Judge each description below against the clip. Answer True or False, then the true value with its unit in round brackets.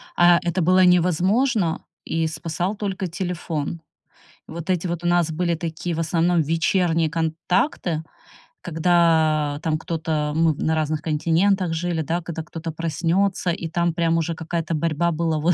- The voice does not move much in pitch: True (1.6 semitones)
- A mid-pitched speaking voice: True (165 Hz)